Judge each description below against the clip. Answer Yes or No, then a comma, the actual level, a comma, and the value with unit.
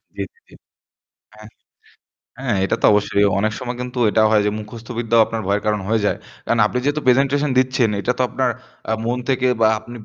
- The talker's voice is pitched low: Yes, low, 120 Hz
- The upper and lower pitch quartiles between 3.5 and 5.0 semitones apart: No, average, 3.1 semitones